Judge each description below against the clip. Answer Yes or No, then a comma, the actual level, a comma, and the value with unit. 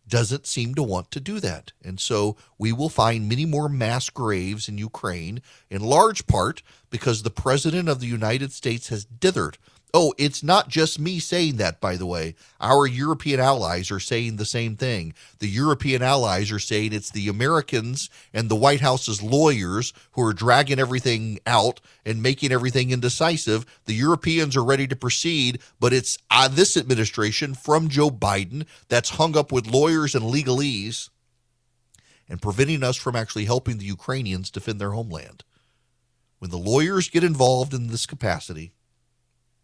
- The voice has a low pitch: Yes, low, 120 Hz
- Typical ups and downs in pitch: Yes, average, 4.3 semitones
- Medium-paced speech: Yes, average, 165 wpm